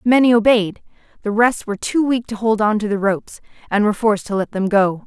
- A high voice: Yes, high, 215 Hz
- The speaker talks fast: Yes, fast, 235 wpm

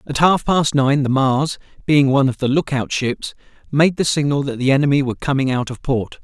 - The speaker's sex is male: Yes, male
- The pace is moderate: No, fast, 230 wpm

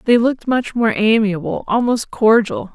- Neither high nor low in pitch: No, high, 225 Hz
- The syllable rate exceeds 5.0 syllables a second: No, 4.7 syllables/s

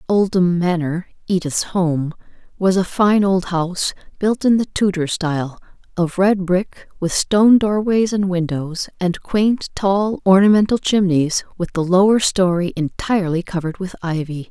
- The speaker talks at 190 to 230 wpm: No, average, 145 wpm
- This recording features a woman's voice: Yes, female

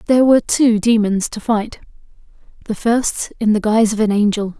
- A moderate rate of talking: Yes, average, 170 wpm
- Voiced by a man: No, female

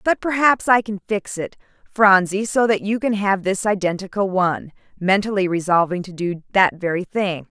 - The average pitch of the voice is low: No, high, 195 Hz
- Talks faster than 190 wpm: No, average, 175 wpm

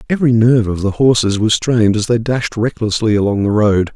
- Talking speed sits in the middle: No, fast, 210 wpm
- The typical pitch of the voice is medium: No, low, 110 Hz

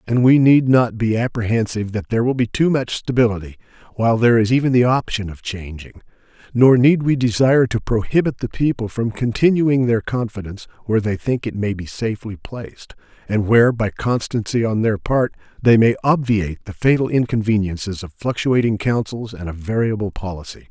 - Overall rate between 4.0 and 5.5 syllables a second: No, 5.7 syllables/s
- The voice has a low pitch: Yes, low, 115 Hz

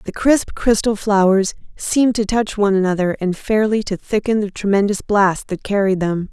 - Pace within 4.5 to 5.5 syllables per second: Yes, 5.1 syllables/s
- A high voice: Yes, high, 205 Hz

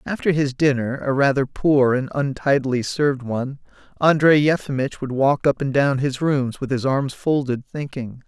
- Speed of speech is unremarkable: Yes, average, 160 wpm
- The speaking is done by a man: Yes, male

